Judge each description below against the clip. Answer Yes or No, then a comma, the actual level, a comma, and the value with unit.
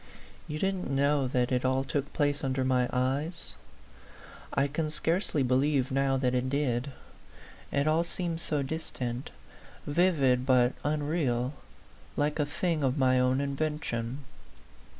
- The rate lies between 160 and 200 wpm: No, slow, 135 wpm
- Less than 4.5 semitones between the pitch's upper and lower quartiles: Yes, average, 2.9 semitones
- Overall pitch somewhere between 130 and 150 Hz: Yes, medium, 140 Hz